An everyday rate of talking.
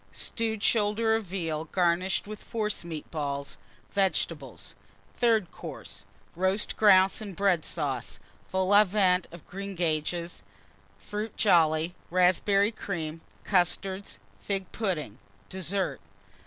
No: slow, 105 wpm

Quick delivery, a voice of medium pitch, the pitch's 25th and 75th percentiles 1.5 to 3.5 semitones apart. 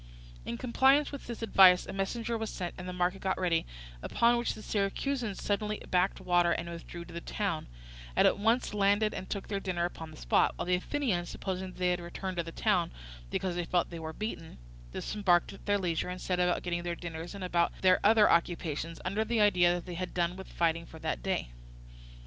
Yes: fast, 215 wpm; medium, 180 Hz; average, 3.1 semitones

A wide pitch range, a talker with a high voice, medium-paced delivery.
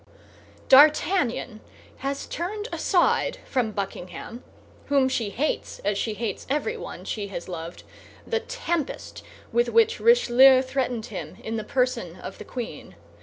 No: wide, 6.4 semitones; very high, 255 Hz; slow, 130 wpm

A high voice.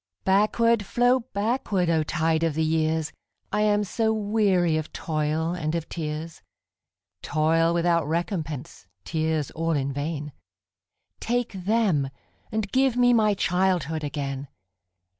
No: medium, 165 Hz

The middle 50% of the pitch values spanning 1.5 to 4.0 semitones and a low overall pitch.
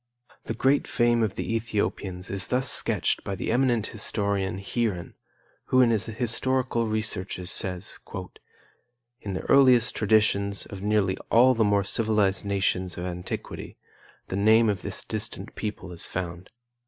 Yes: average, 3.2 semitones; low, 105 Hz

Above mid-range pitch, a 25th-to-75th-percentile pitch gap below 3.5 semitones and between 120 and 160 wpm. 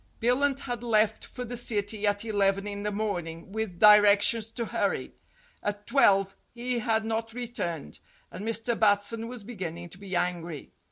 No: high, 210 Hz; narrow, 2.6 semitones; average, 170 wpm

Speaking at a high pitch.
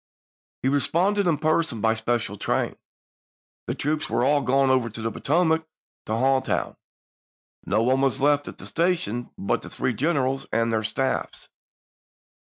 No: low, 135 Hz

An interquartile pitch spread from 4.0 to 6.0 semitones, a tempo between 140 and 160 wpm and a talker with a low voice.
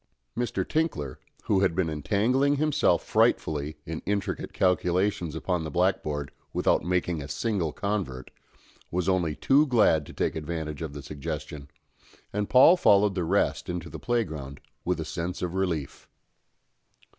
Yes: average, 4.7 semitones; average, 145 wpm; very low, 90 Hz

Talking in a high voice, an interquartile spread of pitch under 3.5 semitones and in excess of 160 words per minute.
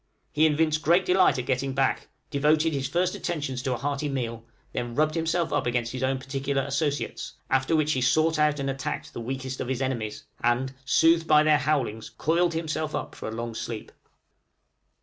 No: medium, 140 Hz; average, 3.1 semitones; average, 190 wpm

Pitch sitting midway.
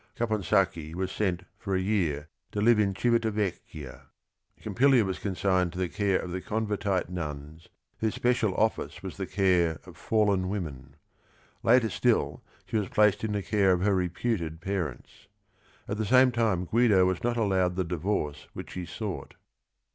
No: very low, 95 Hz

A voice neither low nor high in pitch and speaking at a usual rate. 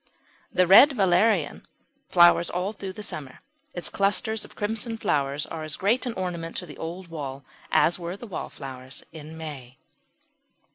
Yes: medium, 175 Hz; average, 155 wpm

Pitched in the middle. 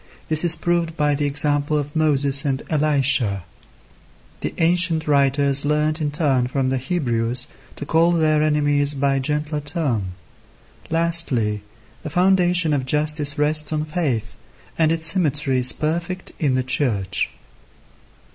Yes: medium, 150 Hz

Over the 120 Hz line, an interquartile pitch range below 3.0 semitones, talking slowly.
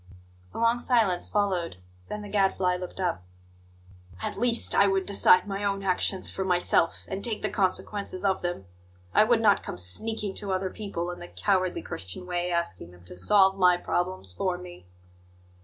No: high, 190 Hz; narrow, 2.4 semitones; average, 175 wpm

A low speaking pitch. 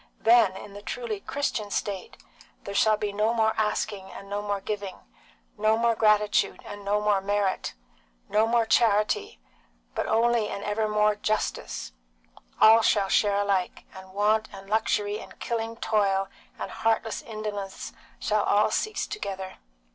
No: high, 210 Hz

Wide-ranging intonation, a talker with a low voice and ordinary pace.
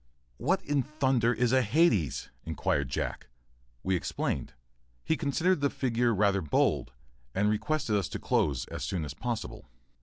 Yes: wide, 6.7 semitones; low, 115 Hz; average, 145 wpm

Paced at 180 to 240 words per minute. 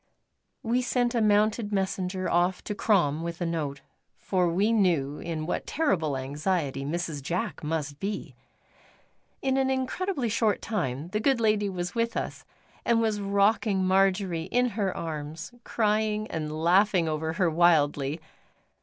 No: average, 145 wpm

